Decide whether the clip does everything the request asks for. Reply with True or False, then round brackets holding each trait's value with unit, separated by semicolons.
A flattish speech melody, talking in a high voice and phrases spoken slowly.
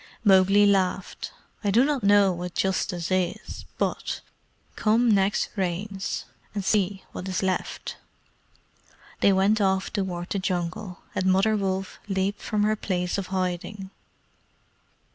True (1.7 semitones; 195 Hz; 130 wpm)